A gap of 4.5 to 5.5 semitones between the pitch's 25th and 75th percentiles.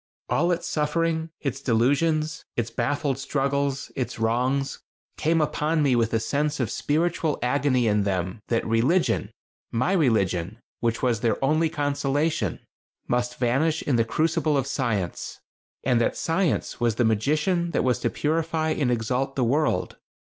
Yes: average, 4.8 semitones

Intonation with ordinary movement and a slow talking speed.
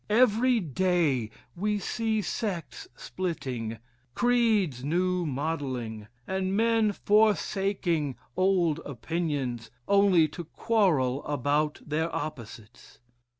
No: wide, 6.4 semitones; slow, 90 wpm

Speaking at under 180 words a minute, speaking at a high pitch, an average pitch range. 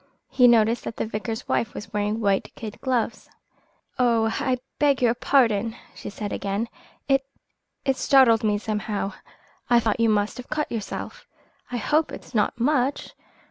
Yes: average, 160 wpm; high, 230 Hz; average, 3.1 semitones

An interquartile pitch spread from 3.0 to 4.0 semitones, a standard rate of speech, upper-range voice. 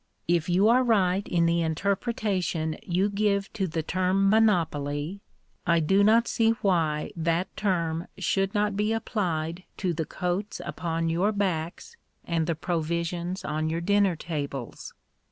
No: average, 3.5 semitones; average, 155 wpm; medium, 180 Hz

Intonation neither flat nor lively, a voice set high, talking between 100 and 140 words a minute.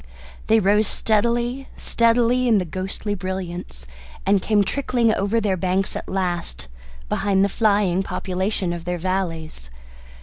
Yes: average, 3.2 semitones; high, 195 Hz; slow, 135 wpm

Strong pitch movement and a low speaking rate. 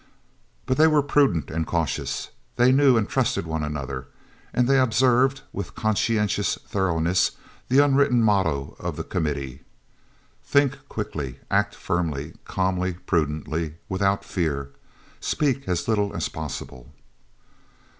Yes: wide, 8.2 semitones; slow, 125 wpm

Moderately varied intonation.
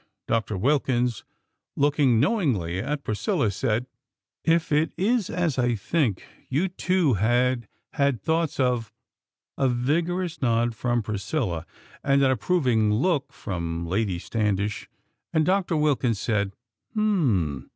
No: wide, 6.5 semitones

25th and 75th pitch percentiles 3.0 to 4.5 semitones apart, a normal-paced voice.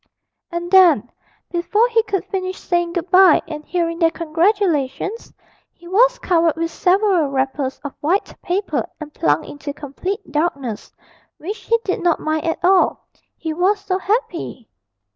Yes: average, 3.9 semitones; average, 150 wpm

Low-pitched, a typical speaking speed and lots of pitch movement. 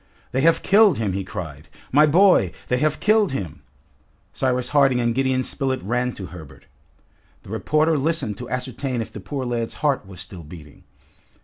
Yes: low, 125 Hz; average, 175 wpm; wide, 6.9 semitones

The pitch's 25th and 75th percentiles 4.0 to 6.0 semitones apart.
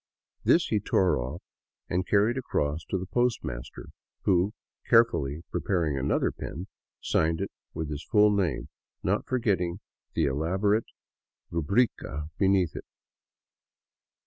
Yes: average, 4.9 semitones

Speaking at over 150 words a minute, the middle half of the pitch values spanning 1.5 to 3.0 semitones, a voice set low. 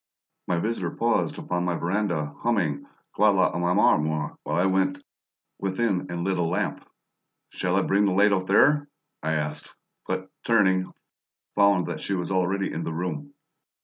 Yes: average, 160 wpm; narrow, 2.6 semitones; very low, 95 Hz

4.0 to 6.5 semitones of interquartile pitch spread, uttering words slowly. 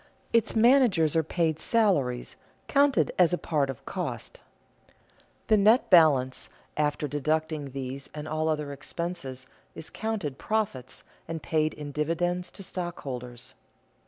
Yes: average, 4.4 semitones; slow, 130 wpm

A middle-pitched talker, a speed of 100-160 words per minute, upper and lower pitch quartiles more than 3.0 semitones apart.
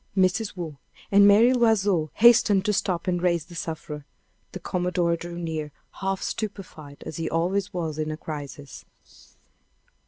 Yes: medium, 175 Hz; average, 150 wpm; average, 3.7 semitones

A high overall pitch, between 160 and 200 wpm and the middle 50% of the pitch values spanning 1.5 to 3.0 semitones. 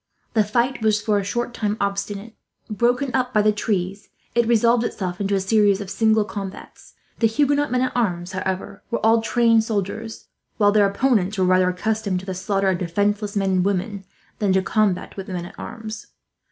Yes: high, 205 Hz; average, 195 wpm; average, 2.7 semitones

